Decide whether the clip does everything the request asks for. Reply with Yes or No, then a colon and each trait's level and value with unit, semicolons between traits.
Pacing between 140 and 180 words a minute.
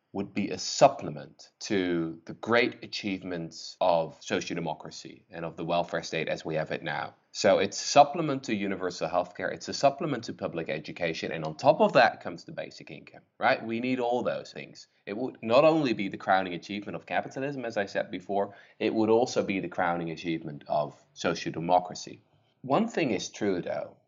No: average, 195 wpm